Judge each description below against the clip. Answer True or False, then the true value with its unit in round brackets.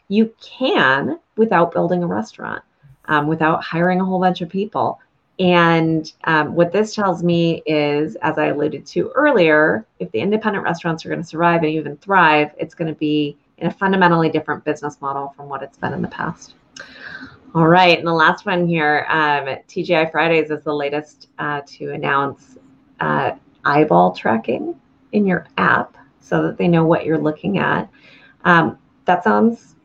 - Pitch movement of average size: True (3.1 semitones)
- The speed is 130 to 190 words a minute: True (175 wpm)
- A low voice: False (160 Hz)